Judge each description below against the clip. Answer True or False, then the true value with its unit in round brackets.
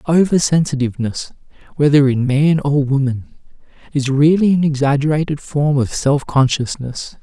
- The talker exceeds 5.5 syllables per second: False (4.8 syllables/s)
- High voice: False (145 Hz)